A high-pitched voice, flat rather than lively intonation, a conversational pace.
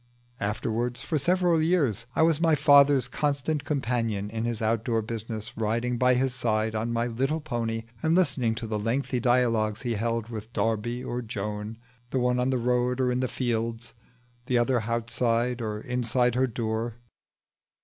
No: low, 120 Hz; narrow, 2.3 semitones; average, 170 wpm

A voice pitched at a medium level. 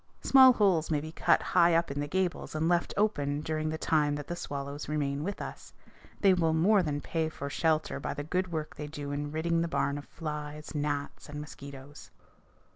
Yes: medium, 155 Hz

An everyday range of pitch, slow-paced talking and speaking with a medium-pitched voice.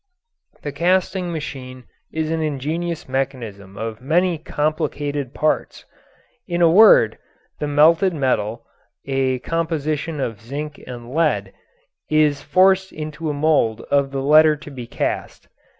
Yes: average, 3.5 semitones; slow, 130 wpm; medium, 150 Hz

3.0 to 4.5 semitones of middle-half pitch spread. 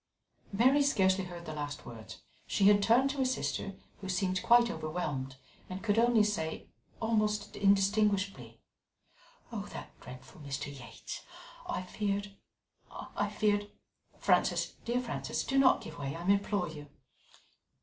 No: average, 5.2 semitones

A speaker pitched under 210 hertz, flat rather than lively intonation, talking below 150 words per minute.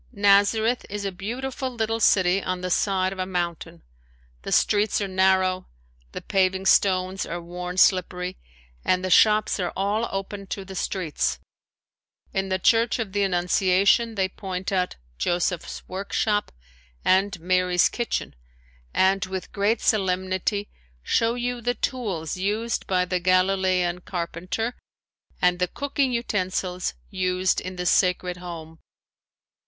Yes: high, 190 Hz; narrow, 2.1 semitones; slow, 135 wpm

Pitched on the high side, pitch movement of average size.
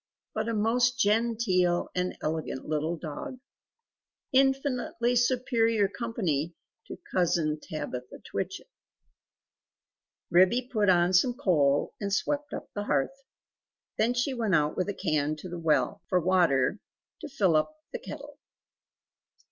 No: high, 200 Hz; wide, 6.6 semitones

